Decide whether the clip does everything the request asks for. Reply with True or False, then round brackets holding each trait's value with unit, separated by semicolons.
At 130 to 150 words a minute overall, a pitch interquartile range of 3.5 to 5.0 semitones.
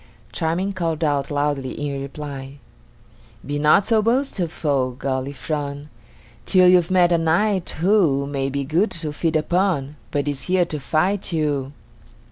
True (140 wpm; 4.1 semitones)